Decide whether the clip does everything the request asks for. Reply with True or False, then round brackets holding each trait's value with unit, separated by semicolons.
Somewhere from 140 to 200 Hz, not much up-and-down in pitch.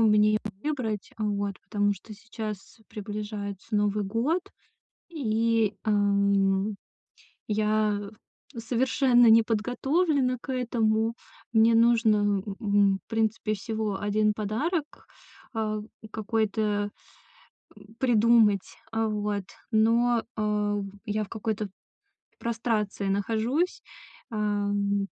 False (215 Hz; 1.9 semitones)